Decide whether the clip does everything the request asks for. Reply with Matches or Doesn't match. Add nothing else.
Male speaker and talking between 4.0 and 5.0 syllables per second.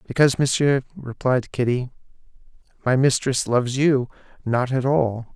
Matches